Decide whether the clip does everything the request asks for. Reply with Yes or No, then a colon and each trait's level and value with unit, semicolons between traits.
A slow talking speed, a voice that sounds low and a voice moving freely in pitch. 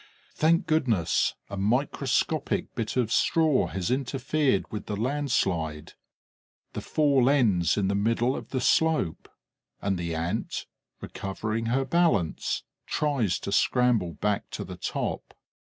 Yes: slow, 130 wpm; low, 115 Hz; wide, 6.1 semitones